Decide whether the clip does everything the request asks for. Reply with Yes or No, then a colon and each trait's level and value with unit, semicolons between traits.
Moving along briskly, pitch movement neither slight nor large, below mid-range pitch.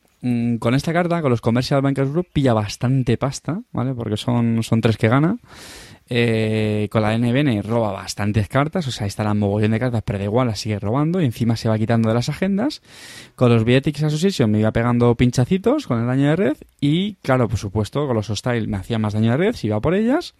Yes: fast, 225 wpm; average, 4.3 semitones; low, 120 Hz